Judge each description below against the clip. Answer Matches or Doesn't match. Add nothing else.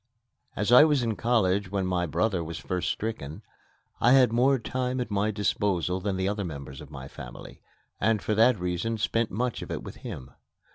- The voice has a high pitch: Doesn't match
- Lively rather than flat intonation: Doesn't match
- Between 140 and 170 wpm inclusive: Doesn't match